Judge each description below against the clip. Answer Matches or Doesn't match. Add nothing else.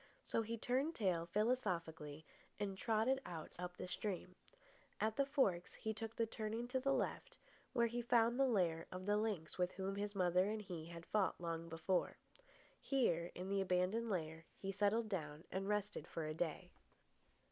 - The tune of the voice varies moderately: Matches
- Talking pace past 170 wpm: Matches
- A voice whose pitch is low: Doesn't match